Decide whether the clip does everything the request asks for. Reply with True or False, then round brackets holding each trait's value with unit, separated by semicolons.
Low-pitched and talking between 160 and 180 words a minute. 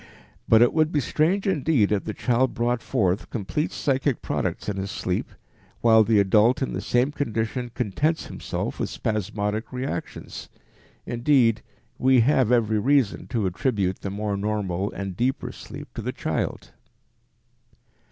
False (115 Hz; 145 wpm)